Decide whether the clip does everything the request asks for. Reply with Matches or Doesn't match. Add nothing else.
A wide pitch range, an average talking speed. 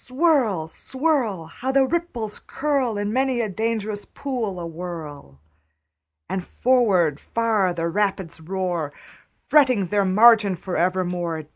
Doesn't match